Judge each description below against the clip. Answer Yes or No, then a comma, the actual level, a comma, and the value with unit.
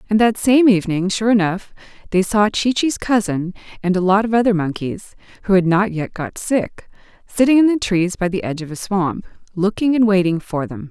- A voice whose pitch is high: Yes, high, 200 Hz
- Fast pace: Yes, fast, 210 wpm